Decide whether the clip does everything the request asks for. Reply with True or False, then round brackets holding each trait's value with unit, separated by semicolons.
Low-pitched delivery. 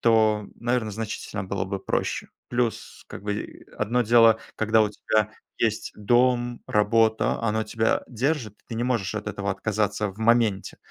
True (110 Hz)